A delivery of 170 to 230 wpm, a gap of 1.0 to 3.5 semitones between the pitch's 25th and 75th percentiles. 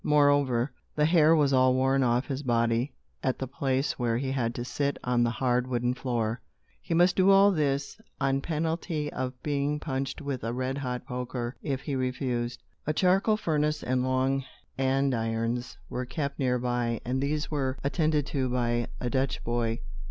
Yes: average, 175 wpm; average, 2.8 semitones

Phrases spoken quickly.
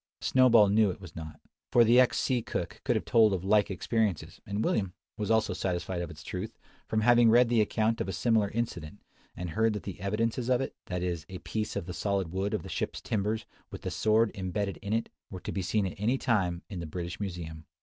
Yes: fast, 230 wpm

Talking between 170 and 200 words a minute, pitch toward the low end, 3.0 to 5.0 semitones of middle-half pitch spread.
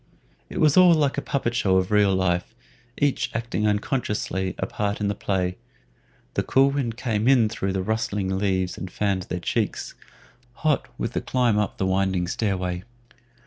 Yes: average, 175 wpm; low, 105 Hz; average, 4.1 semitones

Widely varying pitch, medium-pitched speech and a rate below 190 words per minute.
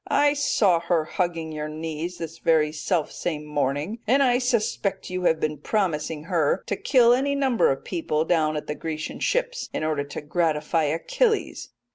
Yes: wide, 6.0 semitones; medium, 165 Hz; average, 175 wpm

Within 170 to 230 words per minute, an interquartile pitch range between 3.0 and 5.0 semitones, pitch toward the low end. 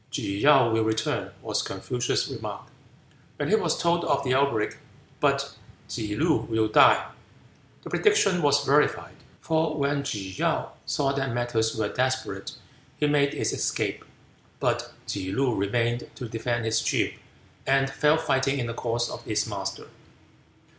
No: average, 155 wpm; average, 4.0 semitones; low, 125 Hz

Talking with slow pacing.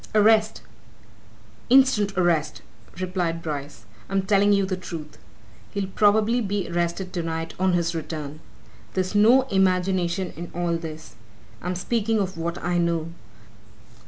Yes: slow, 130 wpm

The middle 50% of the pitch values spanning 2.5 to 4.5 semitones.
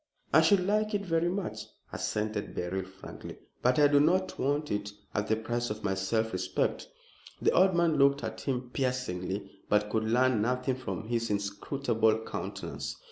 No: wide, 5.6 semitones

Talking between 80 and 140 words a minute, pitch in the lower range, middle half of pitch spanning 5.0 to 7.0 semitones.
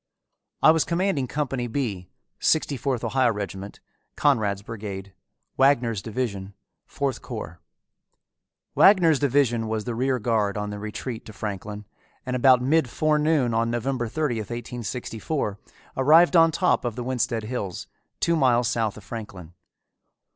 No: slow, 135 wpm; low, 120 Hz; average, 4.5 semitones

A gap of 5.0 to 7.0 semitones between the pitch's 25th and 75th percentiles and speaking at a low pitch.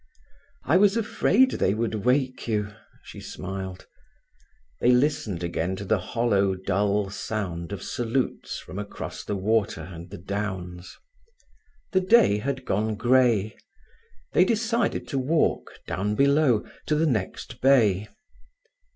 Yes: wide, 5.6 semitones; low, 110 Hz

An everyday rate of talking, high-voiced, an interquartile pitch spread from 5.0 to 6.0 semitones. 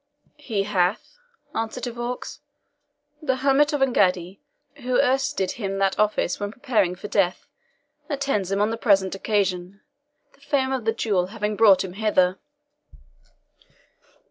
No: average, 145 wpm; high, 210 Hz; average, 4.5 semitones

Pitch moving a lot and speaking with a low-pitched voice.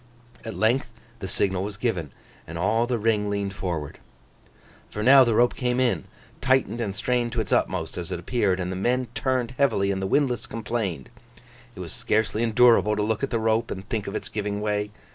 No: average, 3.5 semitones; low, 110 Hz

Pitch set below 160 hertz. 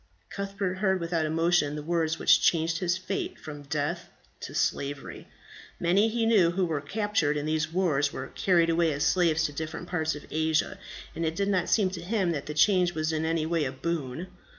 No: medium, 165 Hz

